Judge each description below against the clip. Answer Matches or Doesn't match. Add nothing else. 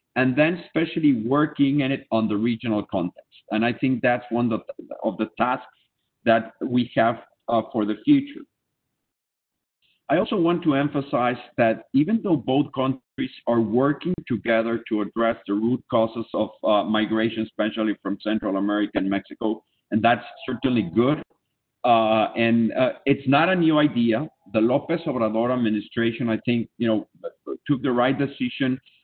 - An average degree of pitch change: Matches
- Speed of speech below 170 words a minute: Matches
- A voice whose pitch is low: Matches